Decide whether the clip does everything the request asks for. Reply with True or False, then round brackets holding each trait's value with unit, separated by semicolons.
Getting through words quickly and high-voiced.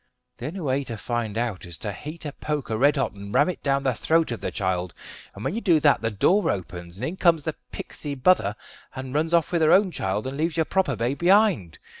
False (245 wpm; 140 Hz)